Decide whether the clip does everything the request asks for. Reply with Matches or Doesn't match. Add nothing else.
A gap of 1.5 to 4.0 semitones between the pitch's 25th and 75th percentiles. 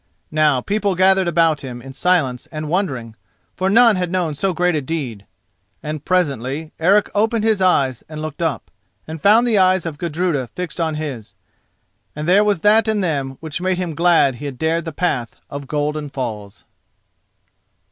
Doesn't match